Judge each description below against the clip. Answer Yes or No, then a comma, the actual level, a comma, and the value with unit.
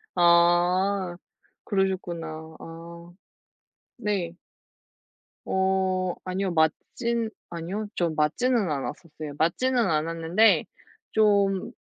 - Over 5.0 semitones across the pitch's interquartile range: No, average, 3.0 semitones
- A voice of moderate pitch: Yes, medium, 180 Hz